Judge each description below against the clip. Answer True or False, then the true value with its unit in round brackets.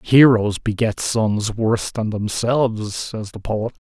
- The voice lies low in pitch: True (110 Hz)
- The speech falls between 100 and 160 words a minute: True (140 wpm)